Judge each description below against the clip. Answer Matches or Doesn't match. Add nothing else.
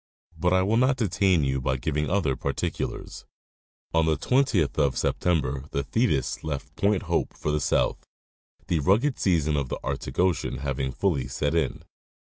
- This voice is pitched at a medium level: Doesn't match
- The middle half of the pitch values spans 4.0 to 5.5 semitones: Matches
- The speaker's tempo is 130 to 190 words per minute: Matches